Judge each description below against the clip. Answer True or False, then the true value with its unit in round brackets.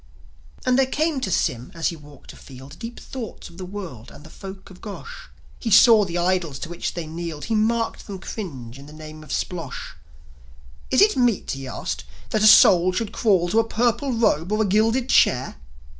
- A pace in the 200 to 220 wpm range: True (205 wpm)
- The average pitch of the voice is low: False (190 Hz)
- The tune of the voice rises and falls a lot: True (6.5 semitones)